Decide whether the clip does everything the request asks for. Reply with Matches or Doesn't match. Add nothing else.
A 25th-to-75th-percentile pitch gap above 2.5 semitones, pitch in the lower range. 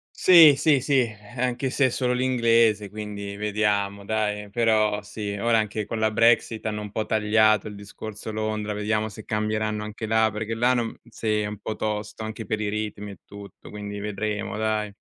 Doesn't match